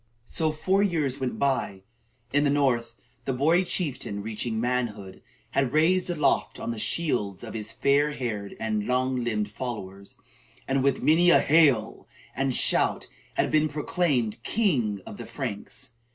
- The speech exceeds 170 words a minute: No, average, 160 wpm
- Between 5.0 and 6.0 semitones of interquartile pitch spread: Yes, wide, 5.4 semitones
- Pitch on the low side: Yes, low, 130 Hz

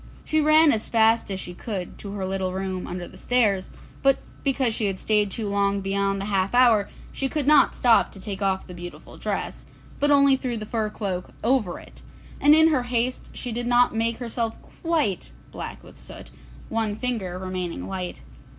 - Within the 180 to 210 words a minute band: Yes, average, 195 wpm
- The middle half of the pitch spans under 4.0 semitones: No, average, 4.4 semitones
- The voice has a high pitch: Yes, high, 215 Hz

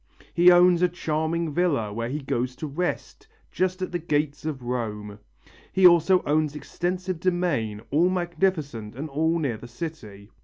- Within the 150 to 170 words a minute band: Yes, average, 160 wpm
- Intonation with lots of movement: Yes, wide, 5.9 semitones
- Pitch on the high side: No, medium, 155 Hz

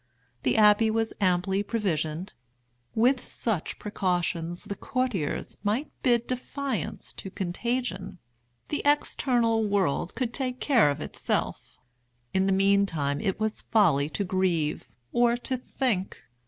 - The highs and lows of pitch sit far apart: No, average, 5.0 semitones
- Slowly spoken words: Yes, slow, 125 wpm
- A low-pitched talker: No, high, 205 Hz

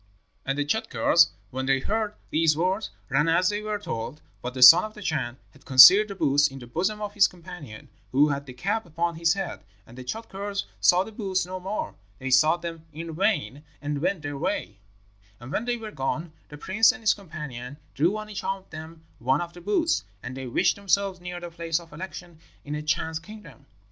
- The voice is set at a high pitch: No, medium, 165 Hz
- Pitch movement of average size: No, wide, 5.7 semitones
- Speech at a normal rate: No, fast, 215 wpm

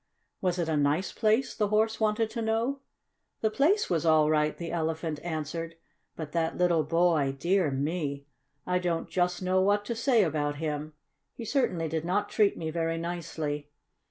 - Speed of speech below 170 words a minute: No, average, 175 wpm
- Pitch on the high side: No, medium, 170 Hz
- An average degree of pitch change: Yes, average, 4.7 semitones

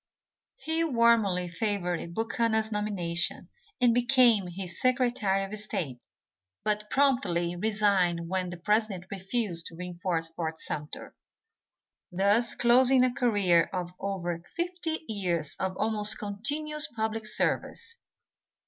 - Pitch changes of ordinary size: Yes, average, 4.9 semitones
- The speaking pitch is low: No, high, 205 Hz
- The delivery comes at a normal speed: No, slow, 110 wpm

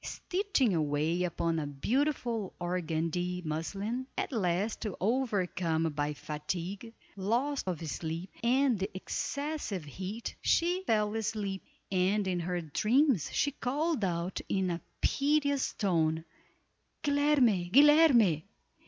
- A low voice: No, high, 195 Hz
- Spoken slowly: Yes, slow, 110 wpm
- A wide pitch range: Yes, wide, 7.2 semitones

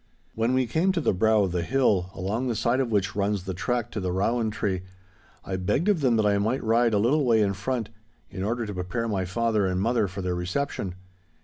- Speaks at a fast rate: Yes, fast, 235 wpm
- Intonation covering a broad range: No, average, 4.0 semitones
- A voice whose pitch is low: Yes, low, 110 Hz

